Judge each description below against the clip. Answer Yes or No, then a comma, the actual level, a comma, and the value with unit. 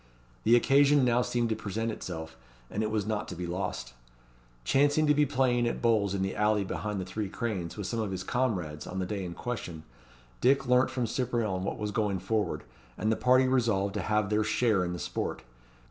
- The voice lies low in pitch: Yes, low, 110 Hz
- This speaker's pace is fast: Yes, fast, 210 wpm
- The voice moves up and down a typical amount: Yes, average, 4.2 semitones